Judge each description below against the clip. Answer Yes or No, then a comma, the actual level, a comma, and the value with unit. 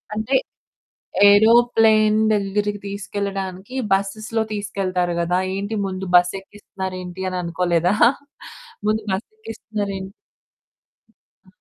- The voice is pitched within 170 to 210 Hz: Yes, high, 200 Hz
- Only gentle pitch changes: Yes, narrow, 2.3 semitones